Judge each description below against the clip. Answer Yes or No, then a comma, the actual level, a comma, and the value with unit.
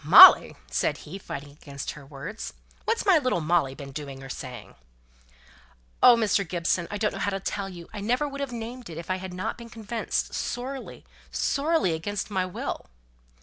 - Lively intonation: Yes, wide, 7.3 semitones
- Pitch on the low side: No, high, 190 Hz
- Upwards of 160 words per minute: Yes, average, 190 wpm